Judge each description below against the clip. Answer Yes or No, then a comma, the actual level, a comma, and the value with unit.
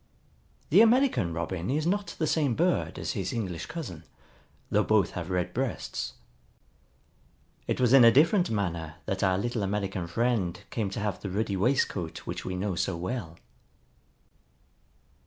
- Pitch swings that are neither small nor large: No, wide, 6.1 semitones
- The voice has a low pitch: Yes, low, 105 Hz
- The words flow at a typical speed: Yes, average, 155 wpm